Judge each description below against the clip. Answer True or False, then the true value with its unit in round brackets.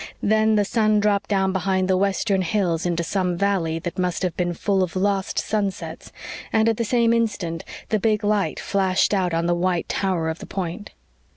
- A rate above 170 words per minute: True (195 wpm)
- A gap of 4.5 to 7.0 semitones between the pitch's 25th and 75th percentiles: False (2.8 semitones)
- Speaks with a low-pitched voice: False (190 Hz)